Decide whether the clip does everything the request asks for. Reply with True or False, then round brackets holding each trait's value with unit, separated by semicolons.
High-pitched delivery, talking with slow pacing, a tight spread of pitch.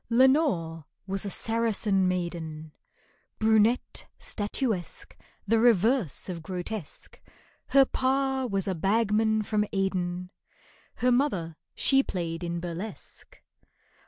False (200 Hz; 100 wpm; 4.8 semitones)